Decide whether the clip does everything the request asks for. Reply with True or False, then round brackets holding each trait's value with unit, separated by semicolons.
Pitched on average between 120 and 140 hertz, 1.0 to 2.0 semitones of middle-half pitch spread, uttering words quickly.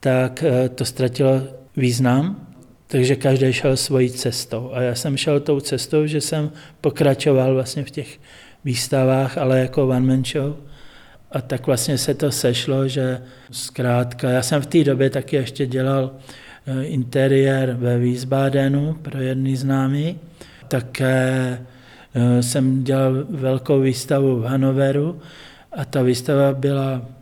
False (135 Hz; 1.7 semitones; 130 wpm)